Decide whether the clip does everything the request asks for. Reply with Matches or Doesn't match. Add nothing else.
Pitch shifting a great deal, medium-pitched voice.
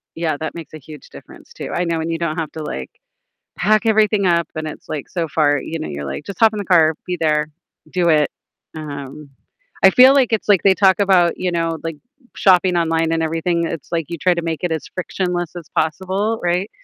Doesn't match